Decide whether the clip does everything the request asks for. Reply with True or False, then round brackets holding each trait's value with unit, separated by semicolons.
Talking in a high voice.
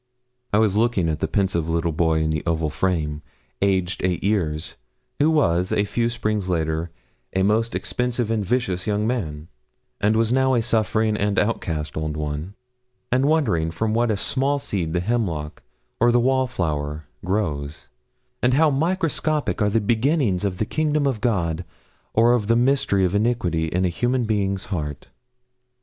False (100 Hz)